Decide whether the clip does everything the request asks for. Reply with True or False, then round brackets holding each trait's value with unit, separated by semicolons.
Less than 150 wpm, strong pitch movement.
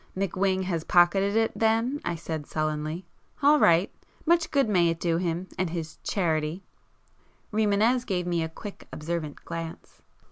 False (140 wpm; 3.9 semitones)